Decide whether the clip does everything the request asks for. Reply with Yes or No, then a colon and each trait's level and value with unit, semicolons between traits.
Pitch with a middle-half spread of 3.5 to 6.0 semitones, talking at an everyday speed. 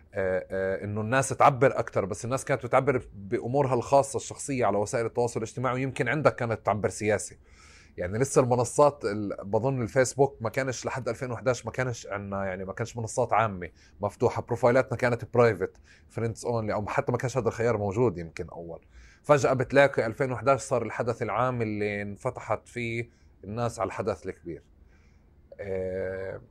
No: average, 4.1 semitones; fast, 155 wpm